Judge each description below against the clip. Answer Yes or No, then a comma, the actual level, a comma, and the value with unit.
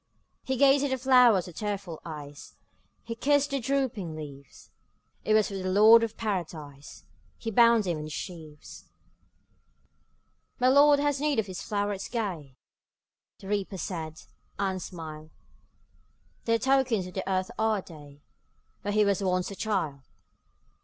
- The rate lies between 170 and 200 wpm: No, average, 155 wpm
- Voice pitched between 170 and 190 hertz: No, high, 200 Hz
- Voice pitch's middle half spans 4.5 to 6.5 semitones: Yes, wide, 5.6 semitones